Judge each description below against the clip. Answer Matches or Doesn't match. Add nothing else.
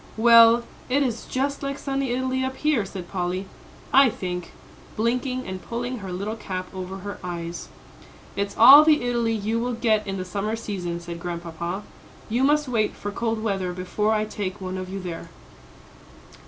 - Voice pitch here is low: Doesn't match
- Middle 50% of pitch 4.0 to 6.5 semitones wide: Matches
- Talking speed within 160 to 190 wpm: Matches